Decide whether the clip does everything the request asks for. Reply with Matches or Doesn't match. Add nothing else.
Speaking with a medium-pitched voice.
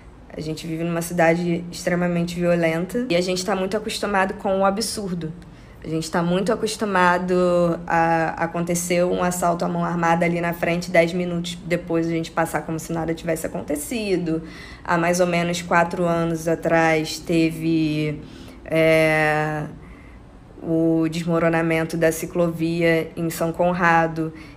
Matches